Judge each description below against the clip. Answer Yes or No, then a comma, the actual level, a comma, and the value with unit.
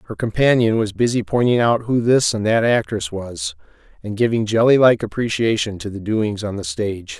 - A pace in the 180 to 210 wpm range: Yes, average, 190 wpm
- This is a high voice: No, low, 110 Hz